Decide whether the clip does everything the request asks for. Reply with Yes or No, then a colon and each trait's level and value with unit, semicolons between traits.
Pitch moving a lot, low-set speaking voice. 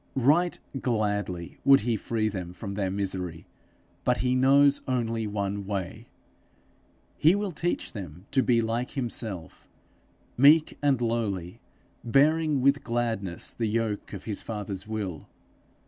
No: average, 4.9 semitones; low, 115 Hz